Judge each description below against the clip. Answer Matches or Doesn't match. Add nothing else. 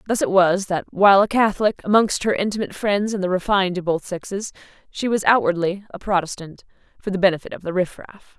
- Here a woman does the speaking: Matches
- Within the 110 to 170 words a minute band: Doesn't match